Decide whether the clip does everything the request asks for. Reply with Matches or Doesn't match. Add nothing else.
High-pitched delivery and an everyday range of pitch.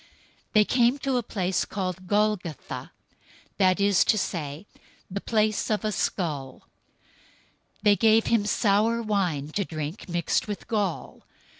Matches